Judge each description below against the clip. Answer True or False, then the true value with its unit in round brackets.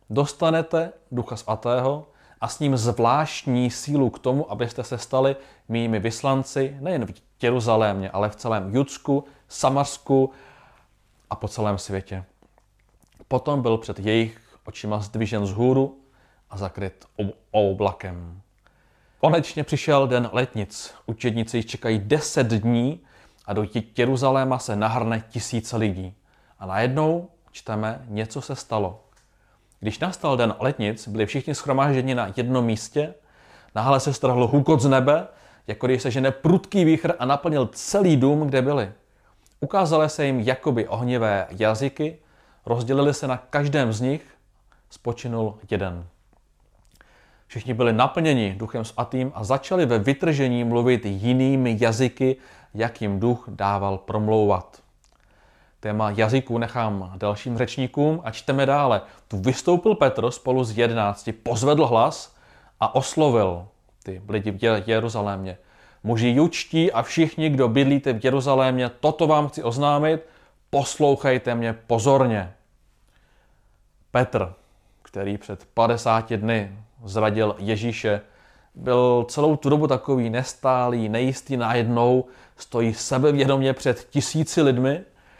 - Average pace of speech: True (125 wpm)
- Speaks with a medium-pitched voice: False (120 Hz)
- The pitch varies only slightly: False (4.1 semitones)